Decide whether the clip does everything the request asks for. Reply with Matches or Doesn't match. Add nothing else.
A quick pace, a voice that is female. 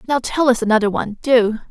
Matches